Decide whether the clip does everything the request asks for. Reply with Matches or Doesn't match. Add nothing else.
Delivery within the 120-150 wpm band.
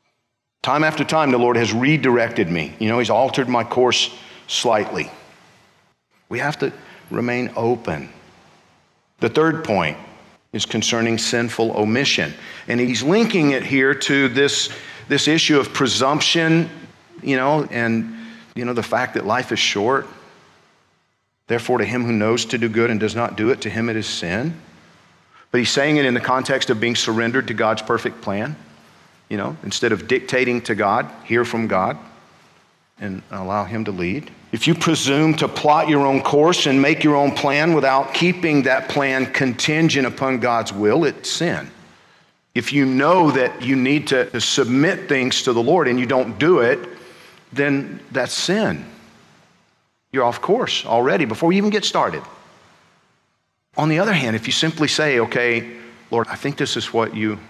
Doesn't match